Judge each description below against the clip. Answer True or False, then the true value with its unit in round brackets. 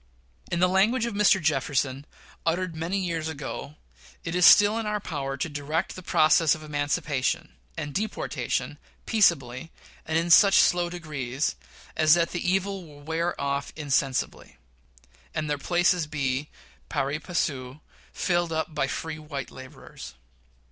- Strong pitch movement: False (3.7 semitones)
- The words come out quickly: False (145 wpm)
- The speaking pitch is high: False (160 Hz)